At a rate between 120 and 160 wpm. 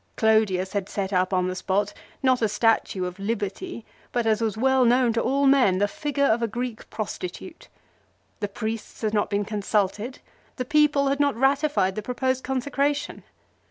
No: average, 180 wpm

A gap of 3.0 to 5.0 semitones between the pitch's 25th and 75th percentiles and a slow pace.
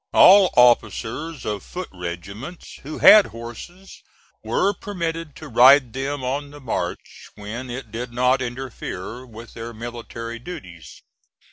Yes: average, 4.3 semitones; slow, 130 wpm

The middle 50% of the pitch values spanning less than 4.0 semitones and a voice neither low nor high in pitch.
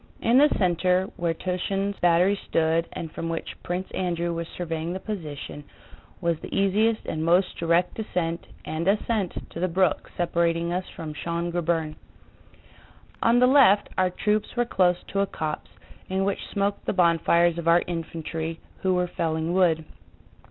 Yes: narrow, 2.5 semitones; medium, 175 Hz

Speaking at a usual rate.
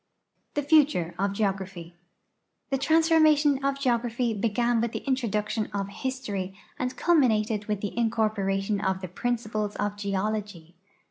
No: slow, 130 wpm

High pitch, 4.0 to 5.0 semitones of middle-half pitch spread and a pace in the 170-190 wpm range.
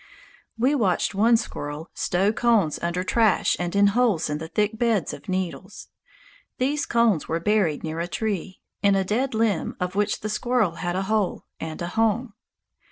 Yes: high, 200 Hz; average, 4.3 semitones; average, 175 wpm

